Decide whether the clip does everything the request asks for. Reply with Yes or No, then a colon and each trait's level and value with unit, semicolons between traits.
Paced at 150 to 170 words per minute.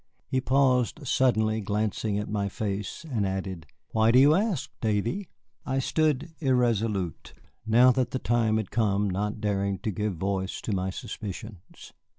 Yes: average, 155 wpm